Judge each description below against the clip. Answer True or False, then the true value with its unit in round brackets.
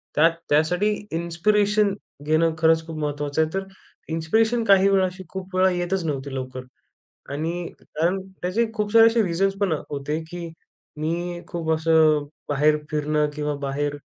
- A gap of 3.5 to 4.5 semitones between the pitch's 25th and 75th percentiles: True (4.1 semitones)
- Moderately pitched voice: True (165 Hz)